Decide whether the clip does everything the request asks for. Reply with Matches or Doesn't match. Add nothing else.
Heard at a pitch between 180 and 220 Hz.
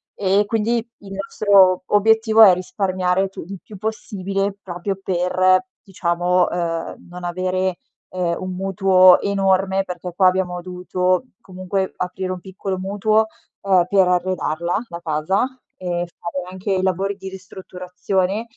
Matches